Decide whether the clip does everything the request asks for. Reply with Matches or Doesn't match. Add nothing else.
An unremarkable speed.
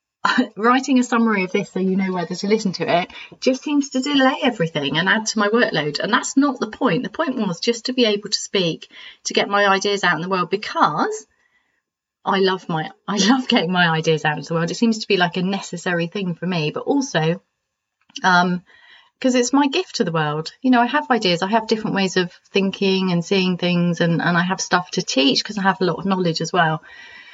Doesn't match